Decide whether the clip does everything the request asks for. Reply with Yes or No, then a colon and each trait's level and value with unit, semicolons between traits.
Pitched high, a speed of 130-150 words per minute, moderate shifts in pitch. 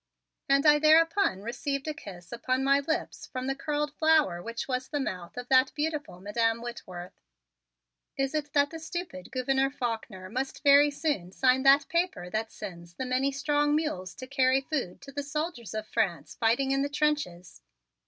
No: very high, 270 Hz; average, 175 wpm; average, 4.6 semitones